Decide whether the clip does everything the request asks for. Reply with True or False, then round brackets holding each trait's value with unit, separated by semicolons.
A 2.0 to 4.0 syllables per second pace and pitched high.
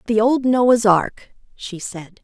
True (3.2 syllables/s; 220 Hz)